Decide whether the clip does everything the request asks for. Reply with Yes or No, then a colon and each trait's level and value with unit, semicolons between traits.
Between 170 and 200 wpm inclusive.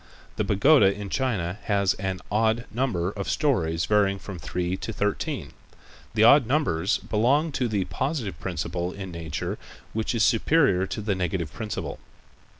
No: average, 150 wpm